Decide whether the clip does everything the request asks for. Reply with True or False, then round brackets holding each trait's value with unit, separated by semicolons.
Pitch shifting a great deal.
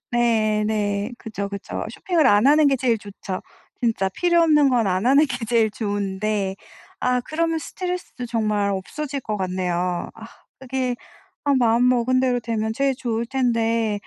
False (3.9 semitones)